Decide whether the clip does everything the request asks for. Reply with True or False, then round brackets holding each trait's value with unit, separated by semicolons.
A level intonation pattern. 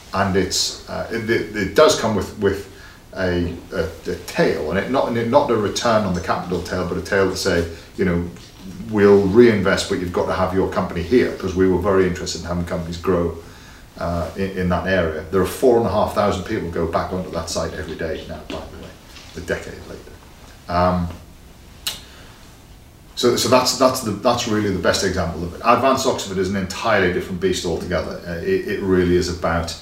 True (2.3 semitones)